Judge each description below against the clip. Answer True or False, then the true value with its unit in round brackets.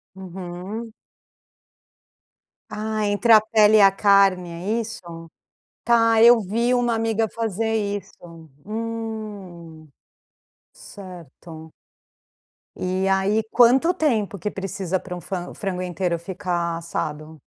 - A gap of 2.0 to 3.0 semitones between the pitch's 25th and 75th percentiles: False (3.9 semitones)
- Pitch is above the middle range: True (195 Hz)